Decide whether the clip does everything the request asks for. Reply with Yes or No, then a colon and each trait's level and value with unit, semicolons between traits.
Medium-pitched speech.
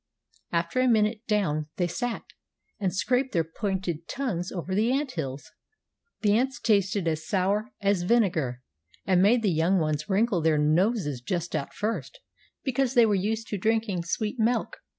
No: high, 195 Hz